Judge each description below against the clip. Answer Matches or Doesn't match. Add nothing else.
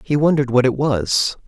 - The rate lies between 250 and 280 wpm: Doesn't match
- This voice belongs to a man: Matches